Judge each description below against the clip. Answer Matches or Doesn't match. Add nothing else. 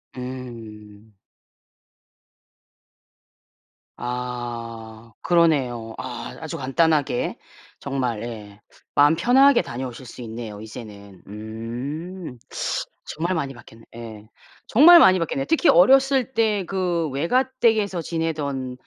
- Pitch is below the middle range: Matches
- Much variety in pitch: Matches